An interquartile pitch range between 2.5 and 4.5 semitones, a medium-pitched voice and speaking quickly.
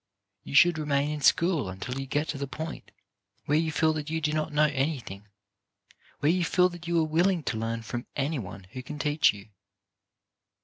Yes: average, 3.3 semitones; medium, 150 Hz; fast, 210 wpm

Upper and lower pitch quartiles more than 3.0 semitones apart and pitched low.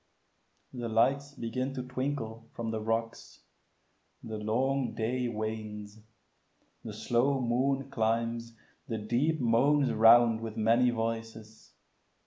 No: narrow, 2.5 semitones; low, 115 Hz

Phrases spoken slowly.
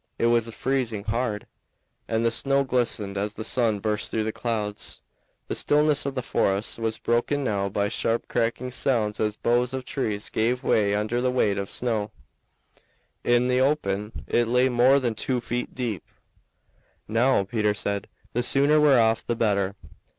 No: average, 170 wpm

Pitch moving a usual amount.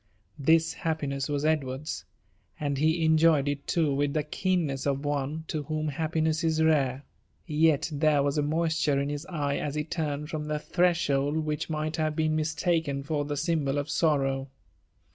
No: narrow, 2.0 semitones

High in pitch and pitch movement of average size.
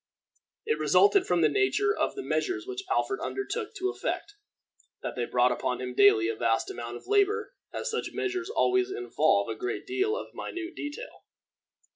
No: very high, 380 Hz; wide, 5.9 semitones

